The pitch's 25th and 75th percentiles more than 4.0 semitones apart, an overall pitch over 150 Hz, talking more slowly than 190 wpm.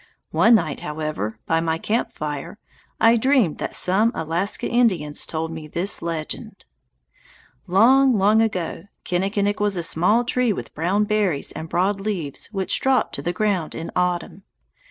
Yes: average, 4.7 semitones; high, 190 Hz; average, 155 wpm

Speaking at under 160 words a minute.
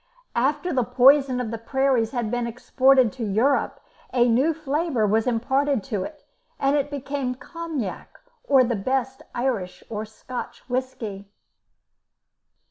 Yes: slow, 135 wpm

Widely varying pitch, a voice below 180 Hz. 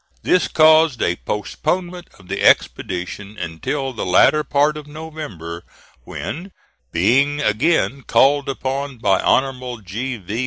Yes: wide, 6.6 semitones; low, 135 Hz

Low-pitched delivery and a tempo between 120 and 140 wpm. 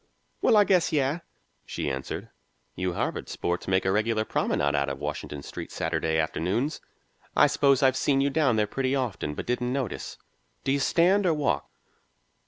No: low, 125 Hz; average, 175 wpm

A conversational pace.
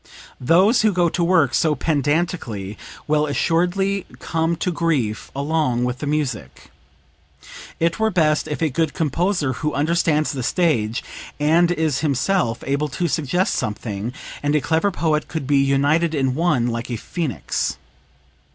Yes: average, 150 wpm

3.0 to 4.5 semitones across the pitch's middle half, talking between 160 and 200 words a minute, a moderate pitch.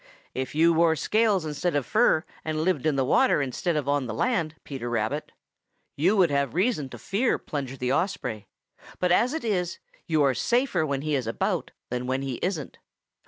No: average, 5.3 semitones; average, 195 wpm; medium, 155 Hz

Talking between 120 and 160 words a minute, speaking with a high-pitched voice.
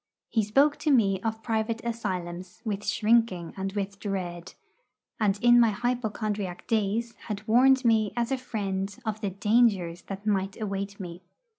Yes: average, 155 wpm; high, 210 Hz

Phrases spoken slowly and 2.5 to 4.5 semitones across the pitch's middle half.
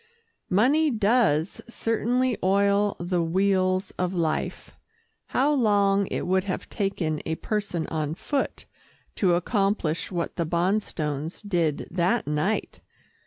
Yes: slow, 120 wpm; average, 3.8 semitones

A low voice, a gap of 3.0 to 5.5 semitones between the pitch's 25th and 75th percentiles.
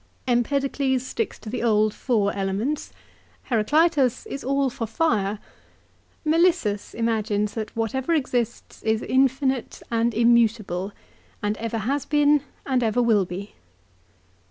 No: high, 235 Hz; average, 4.1 semitones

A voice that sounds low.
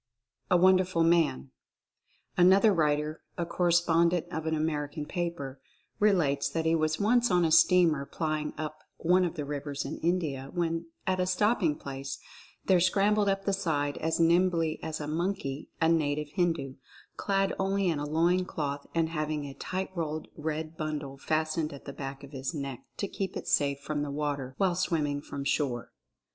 No: medium, 160 Hz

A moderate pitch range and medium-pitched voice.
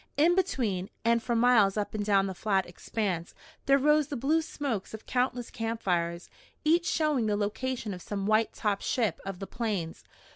No: average, 4.8 semitones; high, 220 Hz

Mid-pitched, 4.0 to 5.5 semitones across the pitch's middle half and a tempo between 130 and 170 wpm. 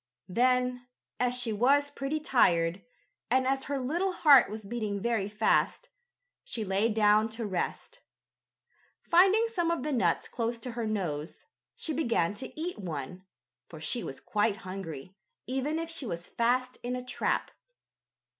No: high, 235 Hz; average, 5.1 semitones; average, 155 wpm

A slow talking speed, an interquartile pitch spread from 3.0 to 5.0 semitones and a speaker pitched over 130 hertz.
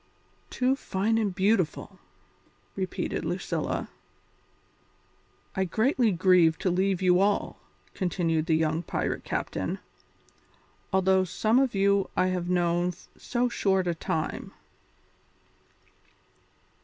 No: slow, 105 wpm; narrow, 2.5 semitones; medium, 185 Hz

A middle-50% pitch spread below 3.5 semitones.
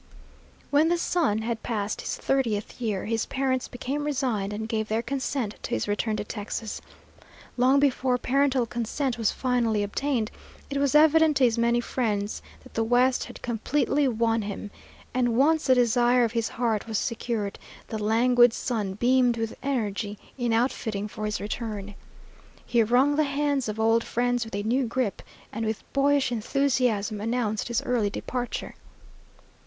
Yes: average, 3.1 semitones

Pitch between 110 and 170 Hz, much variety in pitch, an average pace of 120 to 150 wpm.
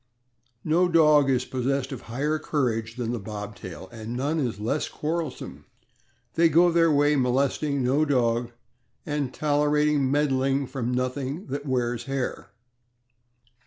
No: low, 135 Hz; average, 3.3 semitones; slow, 135 wpm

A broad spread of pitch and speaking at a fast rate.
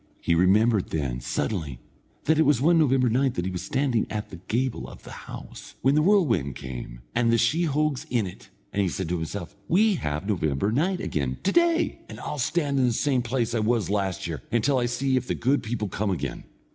Yes: wide, 7.1 semitones; fast, 220 wpm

